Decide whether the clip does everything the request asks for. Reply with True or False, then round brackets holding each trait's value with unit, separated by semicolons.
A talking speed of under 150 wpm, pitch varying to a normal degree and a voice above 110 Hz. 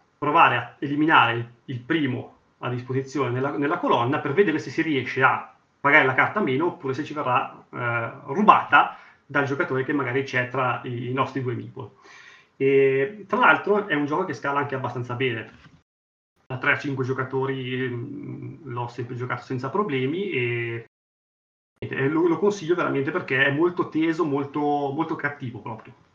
False (165 wpm; 3.1 semitones; 135 Hz)